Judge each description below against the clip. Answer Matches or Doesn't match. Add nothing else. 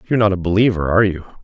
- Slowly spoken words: Doesn't match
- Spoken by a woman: Doesn't match